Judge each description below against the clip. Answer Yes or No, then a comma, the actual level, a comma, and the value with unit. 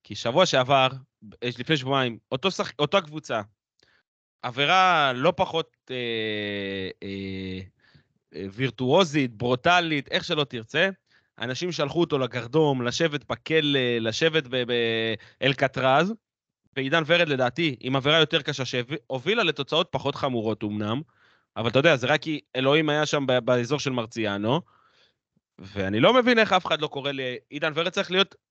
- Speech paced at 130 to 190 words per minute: Yes, average, 140 wpm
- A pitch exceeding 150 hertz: No, low, 135 Hz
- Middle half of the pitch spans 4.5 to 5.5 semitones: Yes, average, 4.9 semitones